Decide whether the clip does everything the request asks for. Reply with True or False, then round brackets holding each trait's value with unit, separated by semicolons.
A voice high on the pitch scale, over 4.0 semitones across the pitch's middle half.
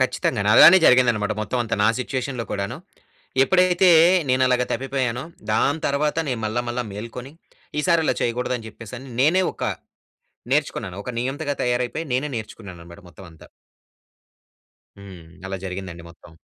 False (125 Hz; 4.7 semitones)